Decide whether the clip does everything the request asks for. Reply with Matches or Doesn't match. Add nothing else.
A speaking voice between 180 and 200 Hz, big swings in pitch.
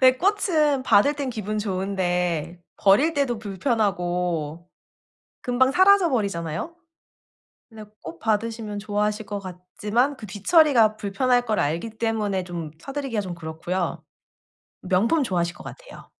Doesn't match